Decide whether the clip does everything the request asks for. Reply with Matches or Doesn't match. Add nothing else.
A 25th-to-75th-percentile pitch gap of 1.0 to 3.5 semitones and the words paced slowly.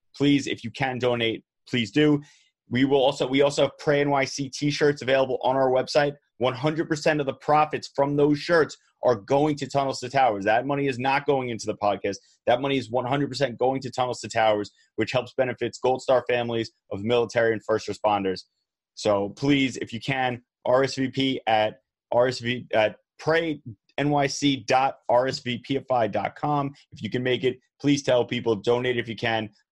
Doesn't match